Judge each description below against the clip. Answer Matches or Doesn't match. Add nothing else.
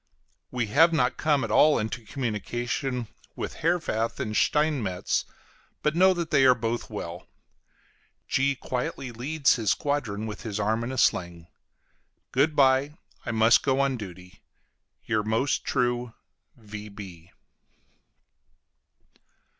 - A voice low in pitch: Matches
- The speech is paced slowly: Matches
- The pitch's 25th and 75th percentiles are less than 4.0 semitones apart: Doesn't match